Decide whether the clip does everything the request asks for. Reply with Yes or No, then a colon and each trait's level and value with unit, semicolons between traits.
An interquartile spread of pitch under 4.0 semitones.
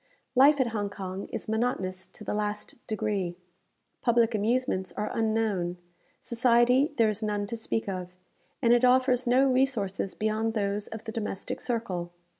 Yes: average, 3.2 semitones